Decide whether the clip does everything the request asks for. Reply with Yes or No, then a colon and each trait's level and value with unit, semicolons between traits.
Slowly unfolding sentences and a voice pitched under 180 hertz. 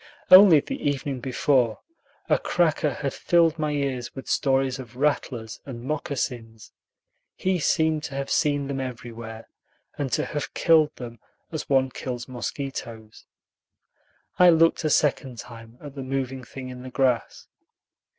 No: average, 145 wpm; low, 135 Hz